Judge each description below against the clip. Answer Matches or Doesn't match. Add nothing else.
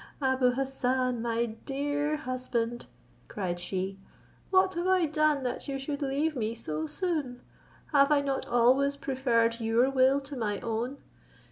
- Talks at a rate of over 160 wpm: Doesn't match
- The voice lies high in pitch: Matches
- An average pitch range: Matches